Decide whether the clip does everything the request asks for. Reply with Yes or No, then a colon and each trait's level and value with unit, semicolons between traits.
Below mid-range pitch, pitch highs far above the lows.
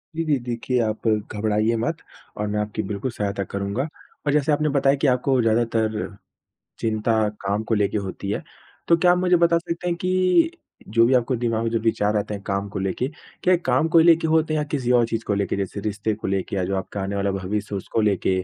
Yes: low, 115 Hz; wide, 5.7 semitones